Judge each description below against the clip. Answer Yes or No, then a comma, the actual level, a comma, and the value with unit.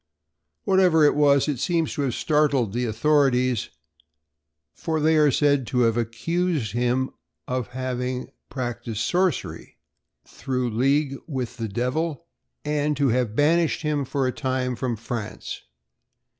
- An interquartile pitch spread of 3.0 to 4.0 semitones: Yes, average, 3.5 semitones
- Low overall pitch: Yes, low, 130 Hz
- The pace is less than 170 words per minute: Yes, slow, 135 wpm